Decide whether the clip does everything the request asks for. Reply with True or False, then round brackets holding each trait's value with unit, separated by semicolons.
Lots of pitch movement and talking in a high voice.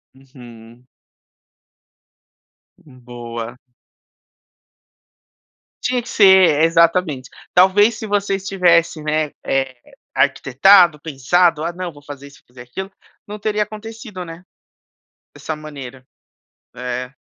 False (6.3 semitones; 160 Hz)